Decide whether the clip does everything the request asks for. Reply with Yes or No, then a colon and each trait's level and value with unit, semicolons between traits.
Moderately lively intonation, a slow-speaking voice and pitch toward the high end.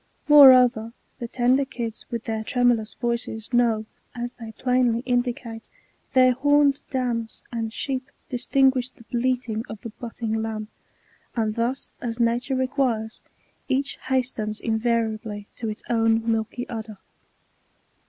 No: narrow, 2.3 semitones; slow, 125 wpm; high, 235 Hz